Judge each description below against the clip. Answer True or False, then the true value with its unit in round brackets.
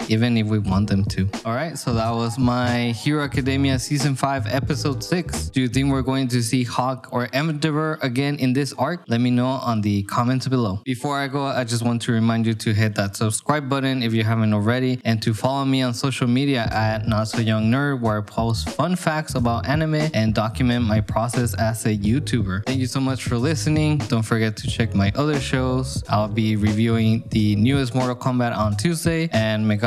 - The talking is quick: True (210 wpm)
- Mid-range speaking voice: False (120 Hz)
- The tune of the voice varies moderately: True (3.4 semitones)